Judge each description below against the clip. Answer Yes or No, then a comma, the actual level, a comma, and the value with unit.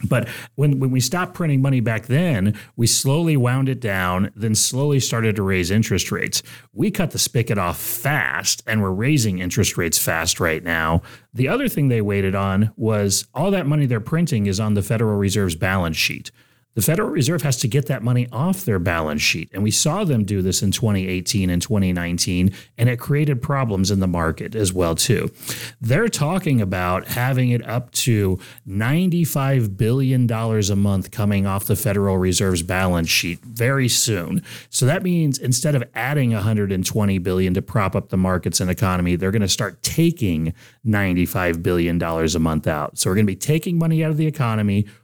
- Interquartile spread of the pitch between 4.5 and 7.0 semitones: Yes, wide, 5.5 semitones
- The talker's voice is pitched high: No, low, 110 Hz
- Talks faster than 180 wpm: Yes, average, 190 wpm